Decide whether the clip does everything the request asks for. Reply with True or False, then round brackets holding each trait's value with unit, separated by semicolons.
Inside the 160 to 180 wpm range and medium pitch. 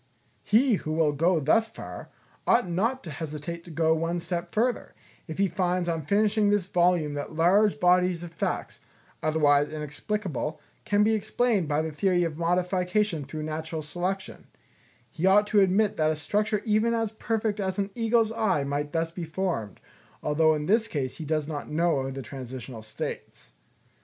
True (170 wpm; 170 Hz)